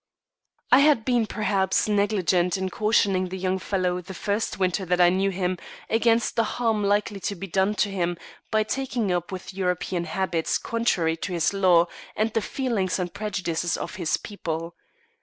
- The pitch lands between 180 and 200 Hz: Yes, high, 190 Hz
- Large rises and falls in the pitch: No, average, 2.9 semitones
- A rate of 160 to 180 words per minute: Yes, average, 170 wpm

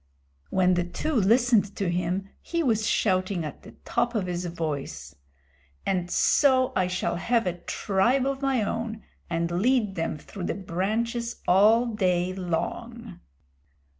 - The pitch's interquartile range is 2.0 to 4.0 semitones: No, average, 4.8 semitones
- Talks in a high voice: Yes, high, 195 Hz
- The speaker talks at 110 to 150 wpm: Yes, average, 145 wpm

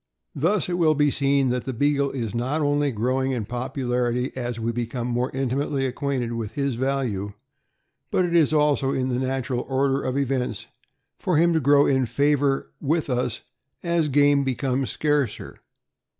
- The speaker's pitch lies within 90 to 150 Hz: Yes, low, 135 Hz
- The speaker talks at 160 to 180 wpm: Yes, average, 165 wpm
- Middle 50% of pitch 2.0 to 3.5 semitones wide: Yes, average, 2.7 semitones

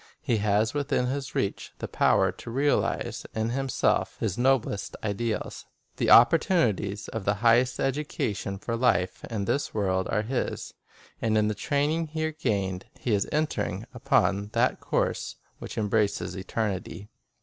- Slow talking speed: No, average, 150 wpm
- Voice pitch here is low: Yes, low, 110 Hz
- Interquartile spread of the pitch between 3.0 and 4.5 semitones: No, average, 4.9 semitones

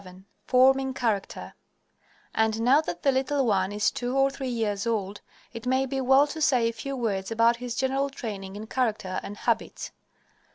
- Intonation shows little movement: No, average, 4.3 semitones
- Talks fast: No, average, 180 wpm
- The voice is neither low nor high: No, high, 235 Hz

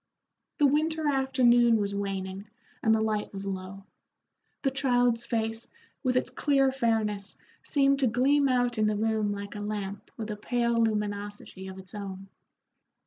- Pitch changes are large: No, average, 3.8 semitones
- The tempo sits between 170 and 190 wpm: No, average, 155 wpm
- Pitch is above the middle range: Yes, high, 220 Hz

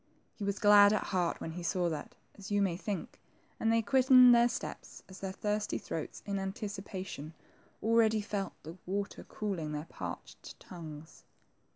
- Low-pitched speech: No, high, 200 Hz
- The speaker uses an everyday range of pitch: Yes, average, 3.3 semitones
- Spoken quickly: No, average, 165 wpm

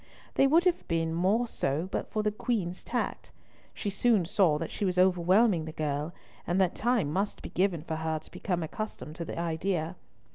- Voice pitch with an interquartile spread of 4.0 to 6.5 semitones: Yes, average, 4.3 semitones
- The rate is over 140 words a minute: Yes, average, 195 wpm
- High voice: No, medium, 180 Hz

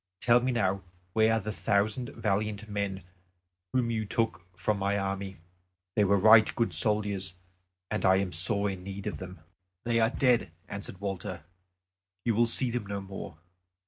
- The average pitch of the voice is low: Yes, low, 100 Hz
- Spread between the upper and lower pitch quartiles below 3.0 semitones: Yes, narrow, 2.6 semitones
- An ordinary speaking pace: Yes, average, 170 wpm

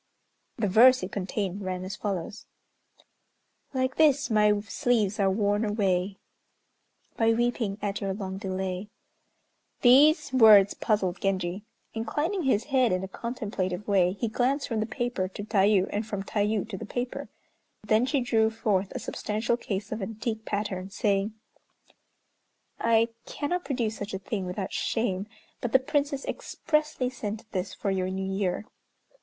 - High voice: Yes, high, 210 Hz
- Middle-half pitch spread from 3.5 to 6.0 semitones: Yes, average, 3.8 semitones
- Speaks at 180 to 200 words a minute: No, average, 150 wpm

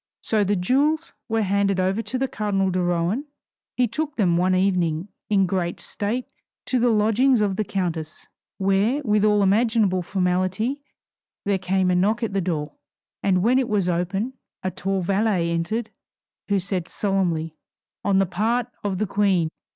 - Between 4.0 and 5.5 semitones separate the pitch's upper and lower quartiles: No, average, 3.3 semitones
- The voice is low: No, high, 195 Hz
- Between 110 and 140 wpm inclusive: No, average, 165 wpm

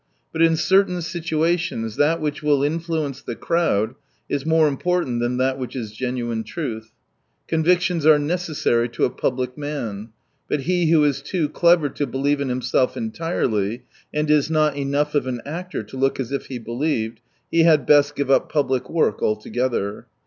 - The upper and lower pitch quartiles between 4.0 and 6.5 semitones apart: Yes, average, 4.5 semitones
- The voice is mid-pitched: Yes, medium, 145 Hz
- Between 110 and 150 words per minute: No, average, 170 wpm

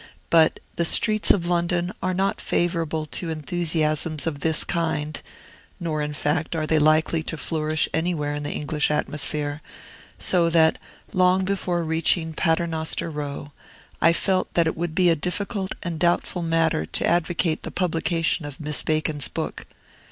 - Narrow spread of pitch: Yes, narrow, 2.1 semitones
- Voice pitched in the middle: Yes, medium, 160 Hz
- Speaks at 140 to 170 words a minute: Yes, average, 155 wpm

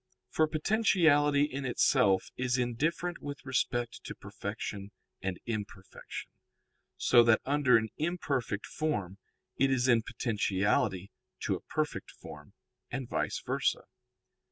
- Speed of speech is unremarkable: No, slow, 120 wpm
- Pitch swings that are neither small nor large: No, wide, 5.7 semitones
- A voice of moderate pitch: No, low, 125 Hz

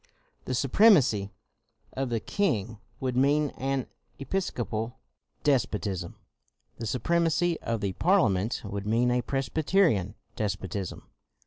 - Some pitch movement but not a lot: No, wide, 5.8 semitones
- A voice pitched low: Yes, low, 125 Hz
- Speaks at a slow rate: Yes, slow, 105 wpm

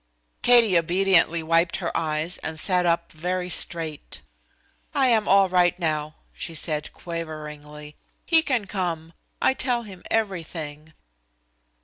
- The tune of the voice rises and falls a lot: No, average, 3.5 semitones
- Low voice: No, medium, 170 Hz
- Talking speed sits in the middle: No, slow, 125 wpm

